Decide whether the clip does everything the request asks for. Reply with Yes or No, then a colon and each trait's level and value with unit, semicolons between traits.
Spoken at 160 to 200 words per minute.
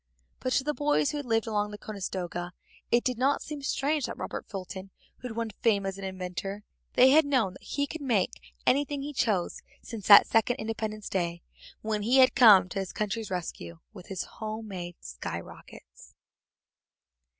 Yes: average, 180 wpm